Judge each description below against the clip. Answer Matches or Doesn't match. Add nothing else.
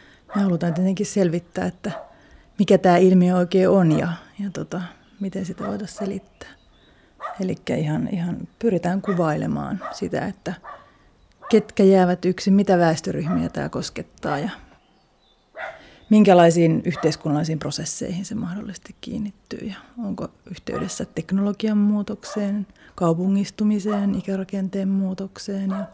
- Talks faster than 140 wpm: Doesn't match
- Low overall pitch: Doesn't match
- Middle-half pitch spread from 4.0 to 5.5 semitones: Doesn't match